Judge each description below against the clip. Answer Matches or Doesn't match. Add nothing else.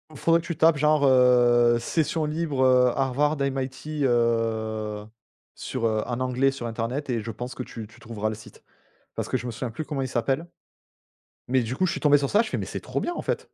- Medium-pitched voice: Doesn't match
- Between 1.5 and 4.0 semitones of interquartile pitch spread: Matches